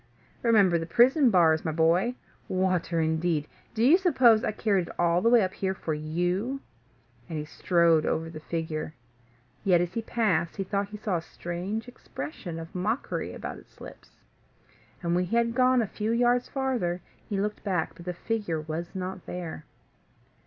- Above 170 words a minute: Yes, average, 180 wpm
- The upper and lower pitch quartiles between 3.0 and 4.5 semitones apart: No, average, 5.2 semitones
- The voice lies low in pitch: No, medium, 185 Hz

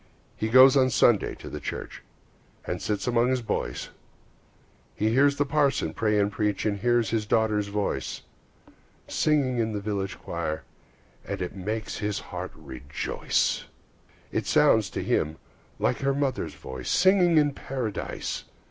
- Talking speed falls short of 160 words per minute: Yes, average, 150 wpm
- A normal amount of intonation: Yes, average, 4.7 semitones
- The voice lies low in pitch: Yes, low, 110 Hz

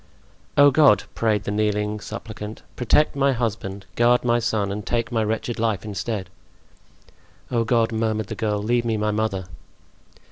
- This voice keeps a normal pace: Yes, average, 155 wpm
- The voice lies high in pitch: No, low, 110 Hz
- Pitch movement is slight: Yes, narrow, 2.1 semitones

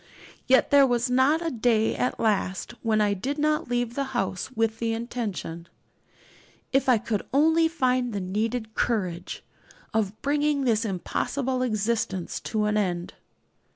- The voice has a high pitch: Yes, high, 235 Hz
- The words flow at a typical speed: Yes, average, 150 wpm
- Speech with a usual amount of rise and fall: Yes, average, 3.8 semitones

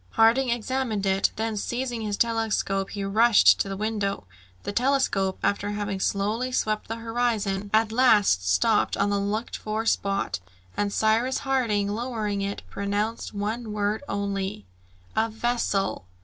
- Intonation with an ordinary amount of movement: No, narrow, 2.3 semitones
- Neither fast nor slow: Yes, average, 145 wpm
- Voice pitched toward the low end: No, high, 215 Hz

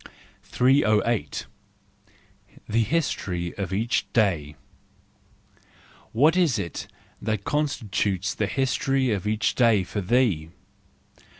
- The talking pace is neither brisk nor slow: No, slow, 100 wpm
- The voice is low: Yes, low, 110 Hz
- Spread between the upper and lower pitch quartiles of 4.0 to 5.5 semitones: Yes, average, 5.1 semitones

